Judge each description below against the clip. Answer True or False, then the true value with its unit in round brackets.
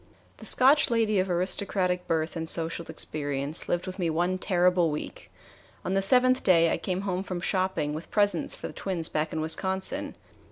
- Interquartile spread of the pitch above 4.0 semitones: False (2.9 semitones)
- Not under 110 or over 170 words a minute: False (185 wpm)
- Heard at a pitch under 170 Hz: False (180 Hz)